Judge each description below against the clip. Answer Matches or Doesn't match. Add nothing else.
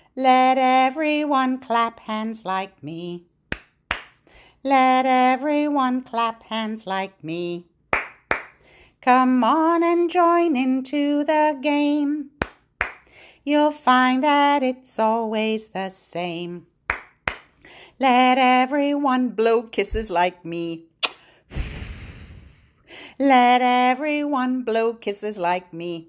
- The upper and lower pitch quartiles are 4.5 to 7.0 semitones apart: Matches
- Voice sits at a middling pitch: Doesn't match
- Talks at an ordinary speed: Doesn't match